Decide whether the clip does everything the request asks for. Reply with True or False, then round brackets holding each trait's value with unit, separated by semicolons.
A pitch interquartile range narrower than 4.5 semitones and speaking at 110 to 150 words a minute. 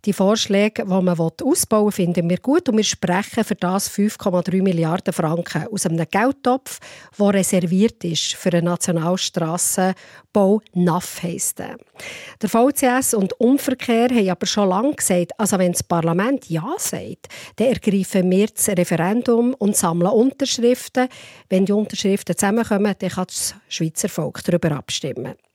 True (3.9 semitones; 145 wpm)